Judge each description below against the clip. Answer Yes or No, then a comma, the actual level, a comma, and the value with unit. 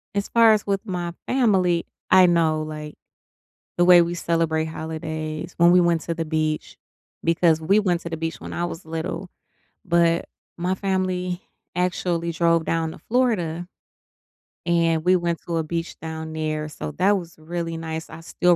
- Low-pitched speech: No, medium, 170 Hz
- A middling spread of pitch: No, narrow, 2.0 semitones